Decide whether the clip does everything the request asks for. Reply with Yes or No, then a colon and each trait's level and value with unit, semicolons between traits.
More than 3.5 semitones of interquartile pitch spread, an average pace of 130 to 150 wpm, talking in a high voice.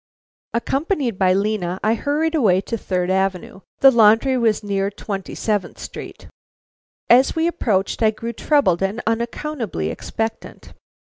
Yes: average, 4.9 semitones; slow, 135 wpm; high, 220 Hz